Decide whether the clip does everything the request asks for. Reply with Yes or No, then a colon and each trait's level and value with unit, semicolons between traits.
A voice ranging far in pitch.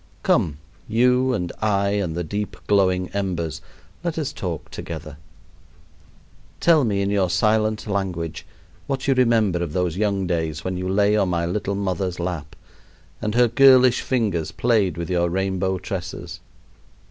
No: average, 3.7 semitones